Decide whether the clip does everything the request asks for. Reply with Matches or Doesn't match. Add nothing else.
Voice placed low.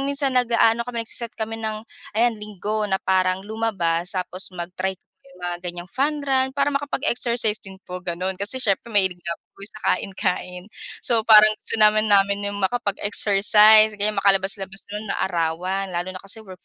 Doesn't match